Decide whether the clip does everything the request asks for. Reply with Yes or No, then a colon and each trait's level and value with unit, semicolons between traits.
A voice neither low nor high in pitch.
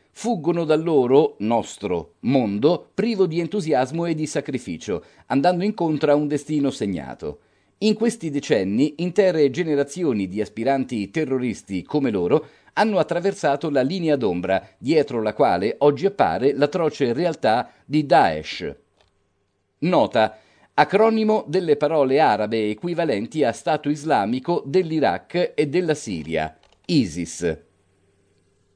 Yes: medium, 145 Hz